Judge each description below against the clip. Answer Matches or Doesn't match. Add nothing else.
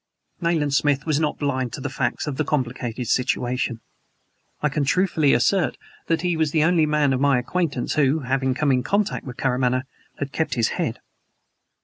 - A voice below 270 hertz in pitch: Matches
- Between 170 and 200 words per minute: Matches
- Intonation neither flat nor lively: Matches